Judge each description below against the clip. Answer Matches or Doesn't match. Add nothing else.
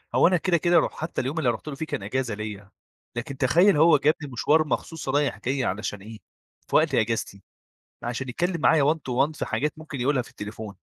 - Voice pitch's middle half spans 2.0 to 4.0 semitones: Doesn't match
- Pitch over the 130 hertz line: Matches